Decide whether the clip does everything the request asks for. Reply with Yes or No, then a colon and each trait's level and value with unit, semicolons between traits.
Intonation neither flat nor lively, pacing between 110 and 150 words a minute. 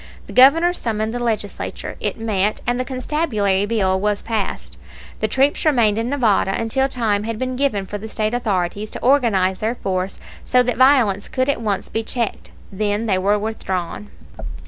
No: average, 3.7 semitones; average, 175 wpm